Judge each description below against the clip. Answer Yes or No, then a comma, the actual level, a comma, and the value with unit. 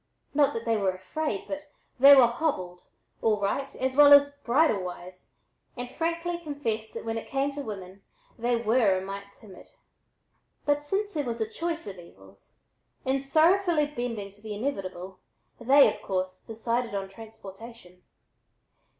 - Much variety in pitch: Yes, wide, 6.4 semitones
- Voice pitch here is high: Yes, high, 230 Hz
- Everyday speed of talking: Yes, average, 160 wpm